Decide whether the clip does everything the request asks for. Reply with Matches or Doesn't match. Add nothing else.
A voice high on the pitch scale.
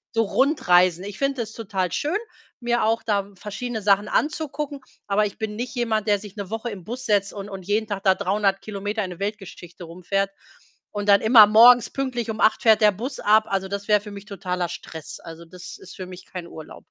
Matches